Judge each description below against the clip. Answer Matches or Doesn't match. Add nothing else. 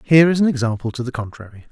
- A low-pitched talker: Matches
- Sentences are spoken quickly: Matches